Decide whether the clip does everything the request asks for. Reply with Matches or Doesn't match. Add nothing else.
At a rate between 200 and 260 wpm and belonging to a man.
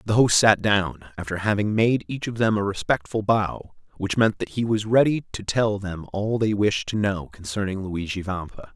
Matches